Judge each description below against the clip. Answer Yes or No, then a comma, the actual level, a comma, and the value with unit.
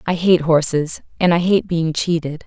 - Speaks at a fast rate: No, average, 195 wpm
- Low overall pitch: No, medium, 165 Hz